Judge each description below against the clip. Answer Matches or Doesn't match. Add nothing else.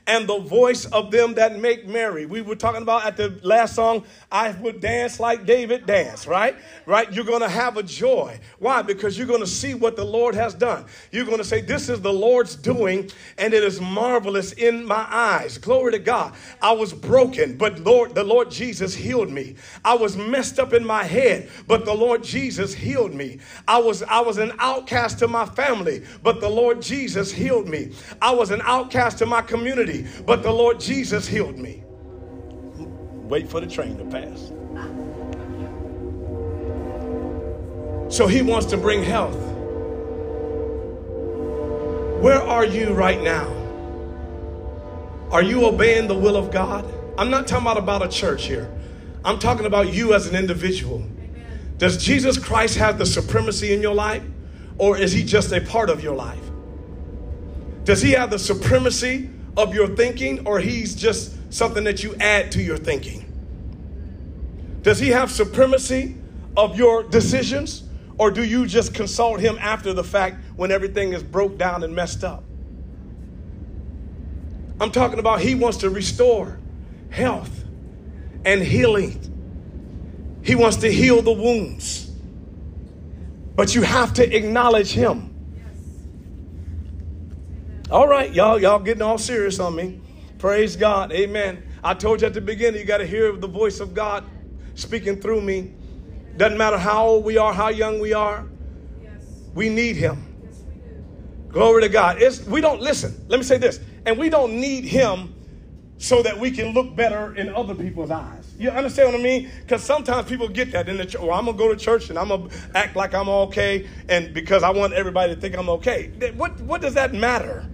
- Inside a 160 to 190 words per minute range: Matches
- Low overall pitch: Doesn't match